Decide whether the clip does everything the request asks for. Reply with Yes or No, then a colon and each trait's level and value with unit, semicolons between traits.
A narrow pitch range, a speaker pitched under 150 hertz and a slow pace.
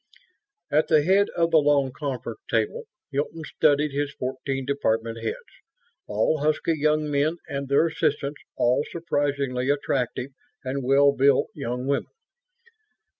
Yes: narrow, 2.3 semitones; medium, 140 Hz; slow, 130 wpm